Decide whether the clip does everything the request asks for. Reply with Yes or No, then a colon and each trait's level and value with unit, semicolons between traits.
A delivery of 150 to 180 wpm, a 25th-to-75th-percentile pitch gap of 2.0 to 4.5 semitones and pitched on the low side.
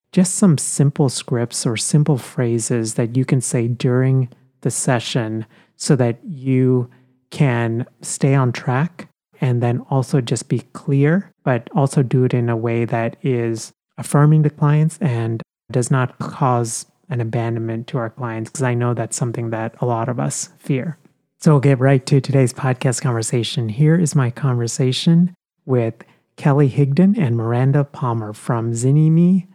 Yes: average, 160 wpm; average, 3.8 semitones; low, 130 Hz